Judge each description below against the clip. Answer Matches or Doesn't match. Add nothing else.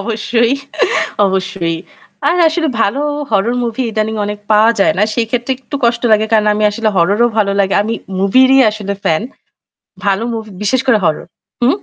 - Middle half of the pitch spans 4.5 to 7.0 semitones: Doesn't match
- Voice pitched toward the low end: Doesn't match